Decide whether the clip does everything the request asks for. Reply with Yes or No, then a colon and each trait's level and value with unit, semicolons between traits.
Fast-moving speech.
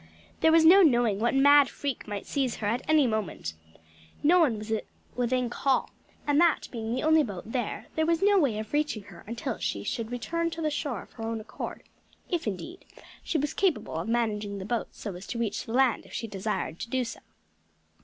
Yes: fast, 215 wpm